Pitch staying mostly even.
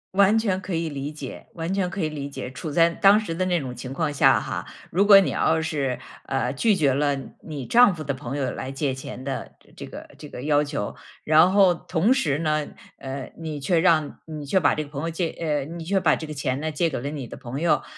No: average, 3.6 semitones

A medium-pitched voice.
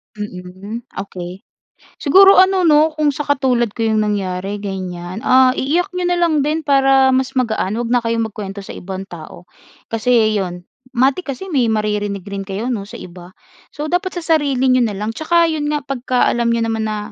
No: high, 235 Hz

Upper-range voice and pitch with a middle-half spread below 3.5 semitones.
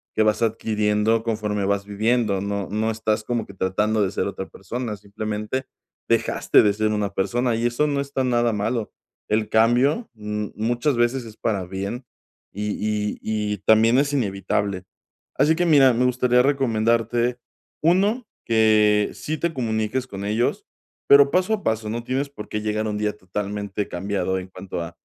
No: low, 110 Hz; average, 2.9 semitones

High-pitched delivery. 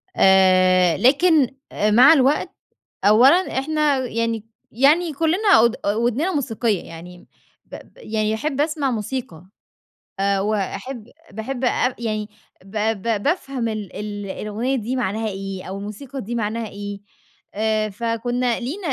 Yes: high, 230 Hz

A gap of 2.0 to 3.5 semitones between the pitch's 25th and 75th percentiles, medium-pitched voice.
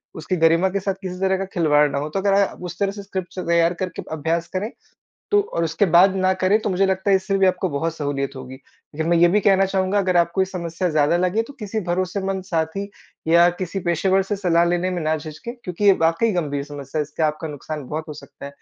Yes: average, 3.2 semitones; medium, 175 Hz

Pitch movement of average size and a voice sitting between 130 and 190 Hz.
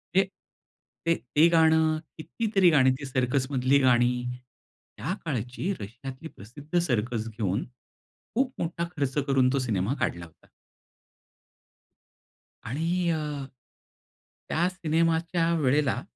Yes: average, 4.8 semitones; medium, 140 Hz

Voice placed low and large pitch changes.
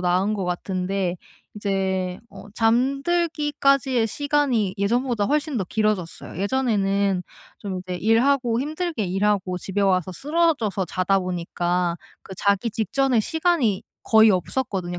No: high, 205 Hz; wide, 6.0 semitones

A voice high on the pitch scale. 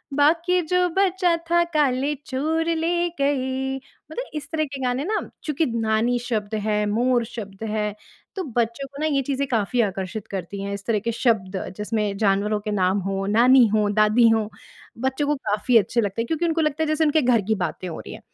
Yes: high, 245 Hz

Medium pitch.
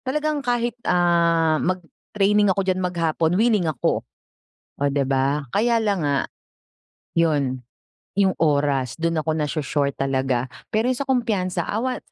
Yes: medium, 170 Hz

